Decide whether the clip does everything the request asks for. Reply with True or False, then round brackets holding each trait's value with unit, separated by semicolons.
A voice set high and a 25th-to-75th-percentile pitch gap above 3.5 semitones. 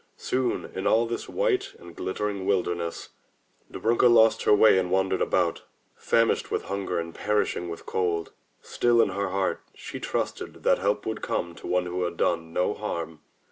False (95 Hz; 4.1 semitones)